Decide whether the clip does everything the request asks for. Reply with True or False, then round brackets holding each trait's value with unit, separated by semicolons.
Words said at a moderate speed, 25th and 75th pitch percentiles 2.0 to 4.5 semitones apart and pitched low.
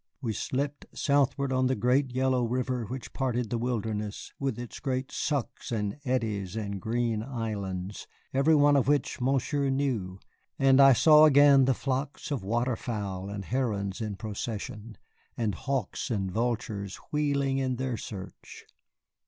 True (145 wpm; 4.2 semitones; 125 Hz)